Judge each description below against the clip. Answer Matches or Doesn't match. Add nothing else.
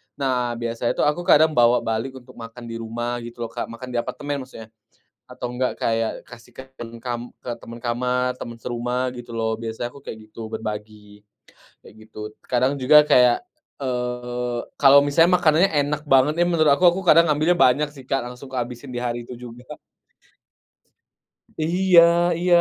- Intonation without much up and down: Doesn't match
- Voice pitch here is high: Doesn't match